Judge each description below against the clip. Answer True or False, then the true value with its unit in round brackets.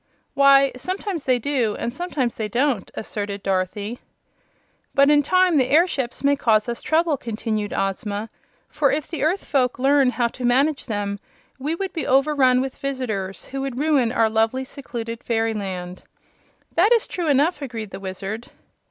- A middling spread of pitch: True (4.7 semitones)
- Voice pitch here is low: False (255 Hz)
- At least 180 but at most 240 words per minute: False (160 wpm)